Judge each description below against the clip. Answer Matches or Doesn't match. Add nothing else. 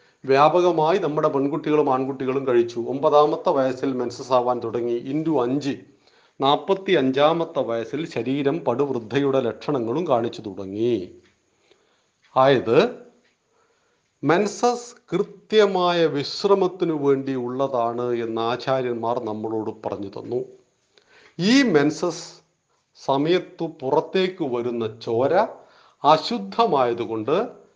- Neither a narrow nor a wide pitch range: Doesn't match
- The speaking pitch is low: Doesn't match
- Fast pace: Doesn't match